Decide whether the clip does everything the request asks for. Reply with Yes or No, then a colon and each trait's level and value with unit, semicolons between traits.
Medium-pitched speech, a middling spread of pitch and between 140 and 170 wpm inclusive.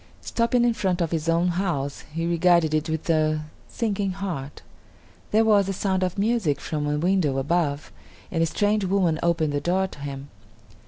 No: medium, 170 Hz; average, 4.1 semitones; average, 180 wpm